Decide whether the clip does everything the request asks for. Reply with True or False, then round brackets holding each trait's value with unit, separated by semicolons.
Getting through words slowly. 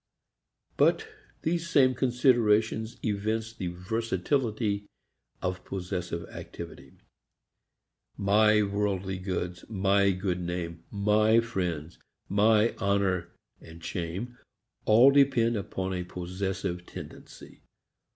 True (95 wpm)